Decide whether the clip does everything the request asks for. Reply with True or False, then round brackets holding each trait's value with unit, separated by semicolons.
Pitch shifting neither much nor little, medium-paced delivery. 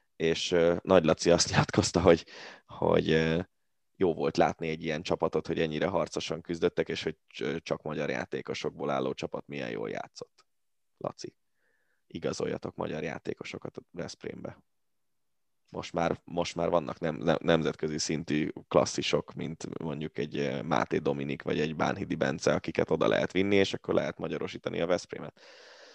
True (3.2 semitones; 145 wpm)